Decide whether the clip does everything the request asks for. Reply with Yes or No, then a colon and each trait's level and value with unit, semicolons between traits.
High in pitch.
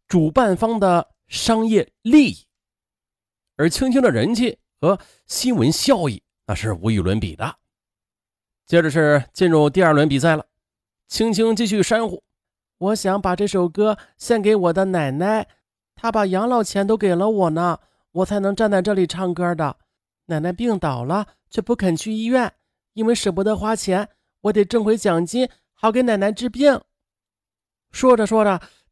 Yes: high, 195 Hz